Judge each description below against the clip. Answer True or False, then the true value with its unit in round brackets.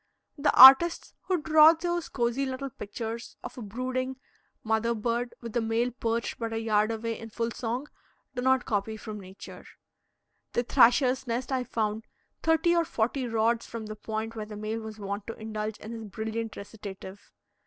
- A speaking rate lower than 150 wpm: False (175 wpm)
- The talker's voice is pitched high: True (230 Hz)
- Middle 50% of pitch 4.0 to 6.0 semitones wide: False (2.8 semitones)